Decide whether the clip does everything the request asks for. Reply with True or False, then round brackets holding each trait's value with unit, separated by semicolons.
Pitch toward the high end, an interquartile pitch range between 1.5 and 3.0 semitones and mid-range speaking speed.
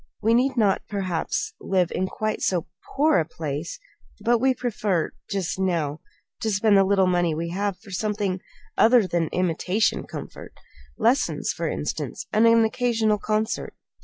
False (200 Hz; 3.8 semitones; 155 wpm)